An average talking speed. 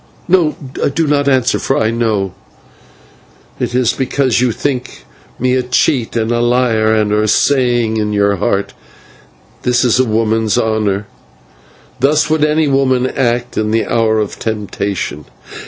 Yes: average, 155 wpm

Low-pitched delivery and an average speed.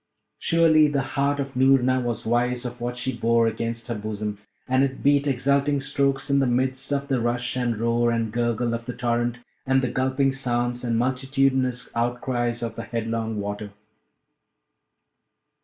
Yes: low, 125 Hz; average, 165 wpm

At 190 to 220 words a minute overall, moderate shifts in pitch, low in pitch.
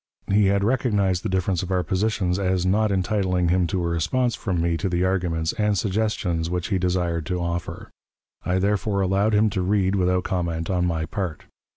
No: average, 195 wpm; narrow, 2.3 semitones; very low, 95 Hz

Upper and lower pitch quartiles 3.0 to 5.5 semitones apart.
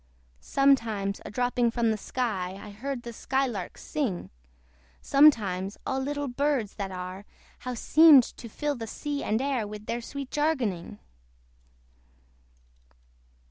Yes: average, 5.1 semitones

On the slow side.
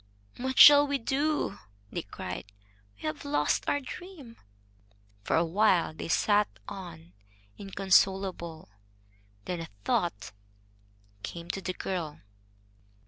Yes: slow, 115 wpm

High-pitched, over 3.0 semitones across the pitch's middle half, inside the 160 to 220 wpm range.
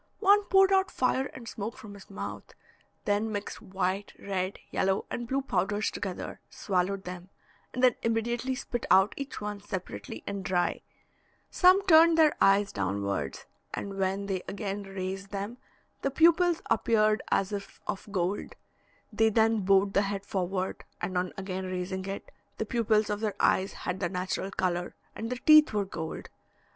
Yes: high, 200 Hz; average, 3.4 semitones; average, 165 wpm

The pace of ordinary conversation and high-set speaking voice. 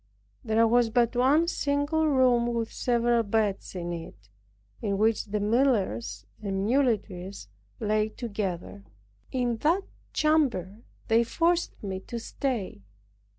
No: slow, 120 wpm; high, 230 Hz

